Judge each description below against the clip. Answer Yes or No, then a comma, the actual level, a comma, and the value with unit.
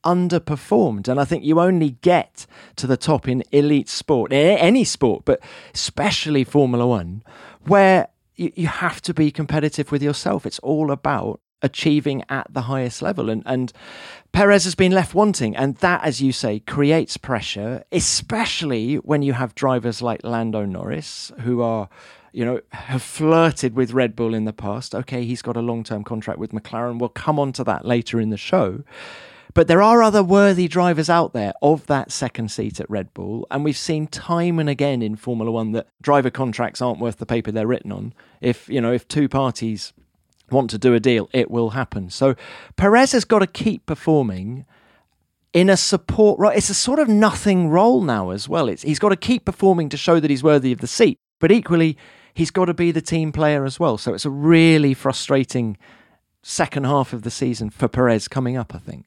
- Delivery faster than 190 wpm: Yes, average, 200 wpm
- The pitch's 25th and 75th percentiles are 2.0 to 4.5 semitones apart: No, wide, 5.6 semitones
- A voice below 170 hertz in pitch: Yes, low, 135 Hz